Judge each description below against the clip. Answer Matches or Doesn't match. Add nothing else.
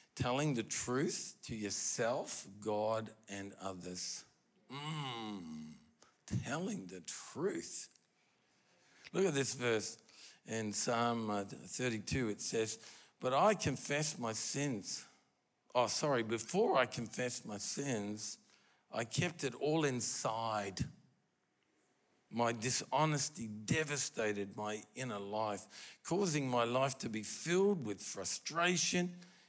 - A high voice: Doesn't match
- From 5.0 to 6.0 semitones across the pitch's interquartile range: Matches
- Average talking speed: Doesn't match